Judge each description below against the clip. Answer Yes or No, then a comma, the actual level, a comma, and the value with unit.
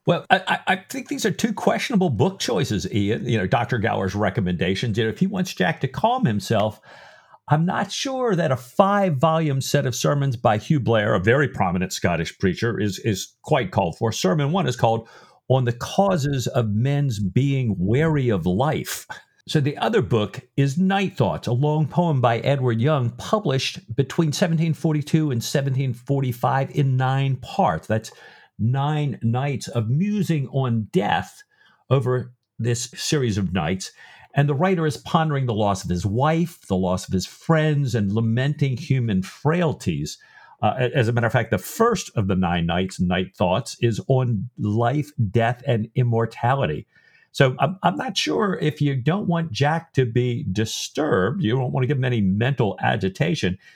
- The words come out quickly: No, average, 170 wpm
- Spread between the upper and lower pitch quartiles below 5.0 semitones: No, average, 5.3 semitones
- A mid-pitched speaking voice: No, low, 130 Hz